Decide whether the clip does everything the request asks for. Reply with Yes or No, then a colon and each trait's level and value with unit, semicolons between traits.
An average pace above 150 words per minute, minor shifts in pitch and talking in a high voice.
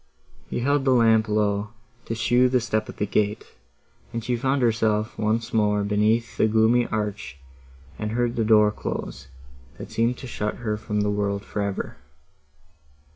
No: average, 170 wpm; narrow, 2.0 semitones; low, 110 Hz